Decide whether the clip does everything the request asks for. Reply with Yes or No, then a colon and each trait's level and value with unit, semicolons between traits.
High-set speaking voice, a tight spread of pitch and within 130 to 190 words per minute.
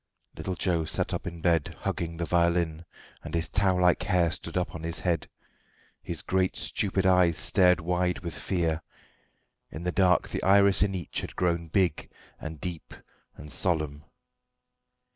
No: very low, 85 Hz; narrow, 1.9 semitones; average, 160 wpm